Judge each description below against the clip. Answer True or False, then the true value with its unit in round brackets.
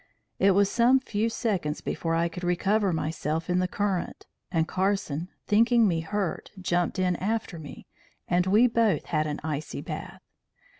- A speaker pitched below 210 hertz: True (185 Hz)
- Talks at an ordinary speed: True (160 wpm)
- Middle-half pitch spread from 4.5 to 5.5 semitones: False (4.0 semitones)